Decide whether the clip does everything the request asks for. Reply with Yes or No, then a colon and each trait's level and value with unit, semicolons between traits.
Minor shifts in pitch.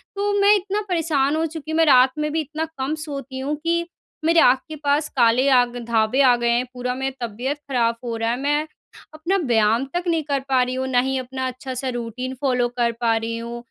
No: average, 3.9 semitones